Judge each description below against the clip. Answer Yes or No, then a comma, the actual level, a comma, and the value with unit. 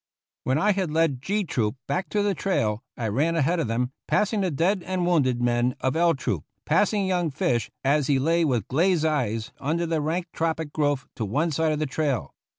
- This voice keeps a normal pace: No, fast, 210 wpm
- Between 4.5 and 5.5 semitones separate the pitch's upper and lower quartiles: Yes, average, 4.9 semitones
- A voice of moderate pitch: Yes, medium, 155 Hz